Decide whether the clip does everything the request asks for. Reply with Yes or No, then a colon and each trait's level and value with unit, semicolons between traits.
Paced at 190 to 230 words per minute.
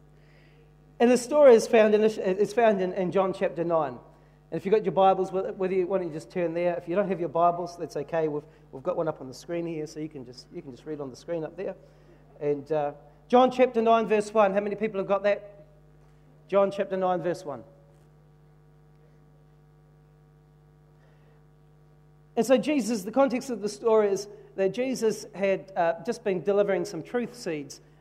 Yes: average, 200 wpm